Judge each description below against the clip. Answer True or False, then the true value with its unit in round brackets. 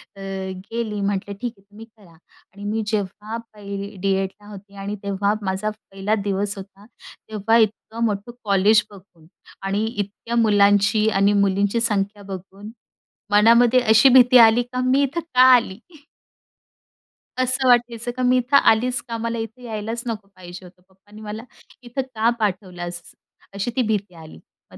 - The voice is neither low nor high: False (210 Hz)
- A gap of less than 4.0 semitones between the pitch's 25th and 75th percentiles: True (2.9 semitones)